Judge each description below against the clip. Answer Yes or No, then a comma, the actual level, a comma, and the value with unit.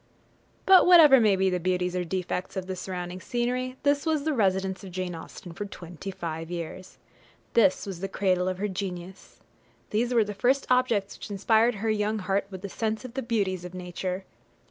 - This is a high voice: Yes, high, 195 Hz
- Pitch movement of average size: Yes, average, 3.8 semitones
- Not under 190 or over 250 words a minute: Yes, average, 200 wpm